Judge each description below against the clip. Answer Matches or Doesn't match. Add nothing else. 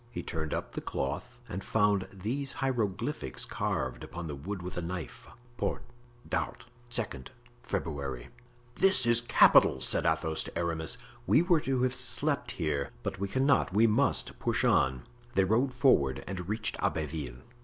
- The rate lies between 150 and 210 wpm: Matches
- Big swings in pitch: Matches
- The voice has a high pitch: Doesn't match